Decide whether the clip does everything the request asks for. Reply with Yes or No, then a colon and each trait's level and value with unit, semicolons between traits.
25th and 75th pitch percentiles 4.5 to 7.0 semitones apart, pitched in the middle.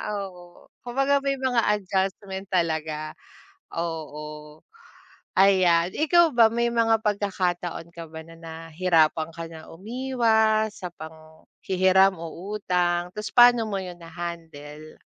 Yes: average, 4.8 semitones; medium, 180 Hz